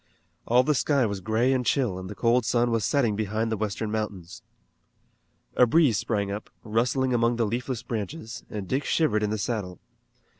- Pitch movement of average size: Yes, average, 3.0 semitones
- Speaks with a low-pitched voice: Yes, low, 115 Hz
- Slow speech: No, average, 185 wpm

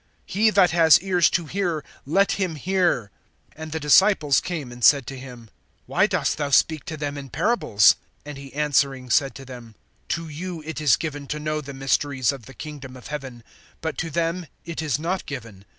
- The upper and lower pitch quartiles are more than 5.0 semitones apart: No, average, 3.6 semitones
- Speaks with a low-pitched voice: No, medium, 150 Hz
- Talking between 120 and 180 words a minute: No, average, 200 wpm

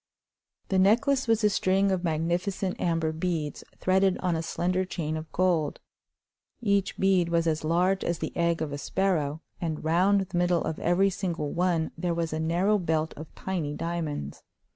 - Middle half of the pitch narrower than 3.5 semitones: Yes, average, 2.9 semitones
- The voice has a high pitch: No, medium, 175 Hz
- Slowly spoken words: No, average, 175 wpm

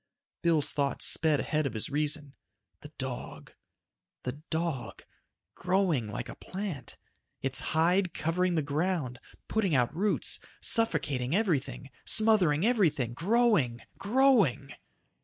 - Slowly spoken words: Yes, slow, 115 wpm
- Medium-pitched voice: Yes, medium, 160 Hz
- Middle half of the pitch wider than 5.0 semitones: Yes, wide, 5.6 semitones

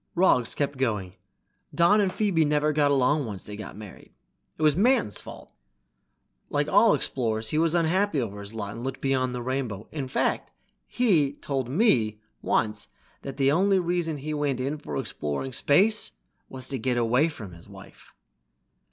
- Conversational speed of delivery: Yes, average, 170 wpm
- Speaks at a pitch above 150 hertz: No, low, 135 Hz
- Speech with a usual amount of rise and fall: No, wide, 5.7 semitones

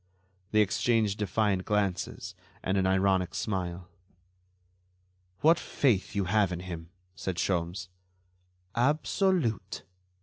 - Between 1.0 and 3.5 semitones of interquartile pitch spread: Yes, average, 2.9 semitones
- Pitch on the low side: Yes, low, 100 Hz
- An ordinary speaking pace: No, slow, 100 wpm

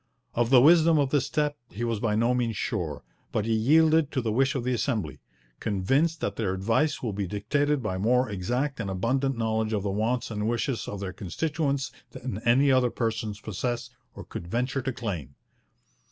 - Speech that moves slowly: No, average, 195 wpm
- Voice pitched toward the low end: Yes, low, 120 Hz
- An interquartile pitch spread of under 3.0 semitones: No, average, 4.3 semitones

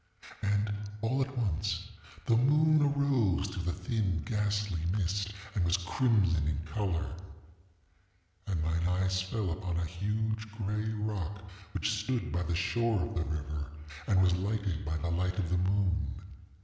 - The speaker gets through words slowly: No, average, 155 wpm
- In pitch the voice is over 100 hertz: No, very low, 95 Hz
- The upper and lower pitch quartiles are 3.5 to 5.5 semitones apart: Yes, average, 3.8 semitones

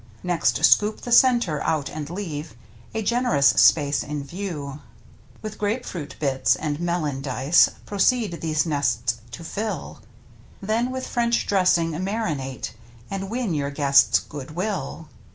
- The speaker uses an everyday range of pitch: No, wide, 6.3 semitones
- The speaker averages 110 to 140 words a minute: Yes, slow, 135 wpm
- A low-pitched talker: No, medium, 165 Hz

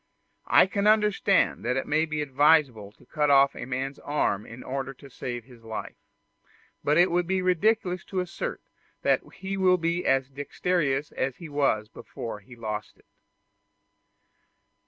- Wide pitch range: Yes, wide, 5.7 semitones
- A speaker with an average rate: Yes, average, 160 wpm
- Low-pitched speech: No, medium, 145 Hz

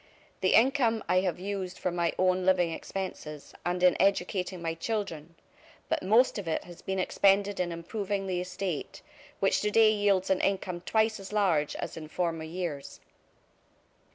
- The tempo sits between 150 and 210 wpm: Yes, average, 160 wpm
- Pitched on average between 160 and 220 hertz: Yes, medium, 185 Hz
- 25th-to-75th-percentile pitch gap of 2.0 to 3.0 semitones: Yes, narrow, 2.6 semitones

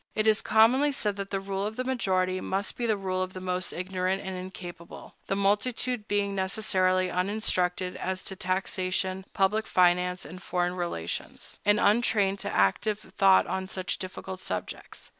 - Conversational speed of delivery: Yes, average, 165 wpm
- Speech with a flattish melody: Yes, narrow, 2.0 semitones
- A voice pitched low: No, high, 190 Hz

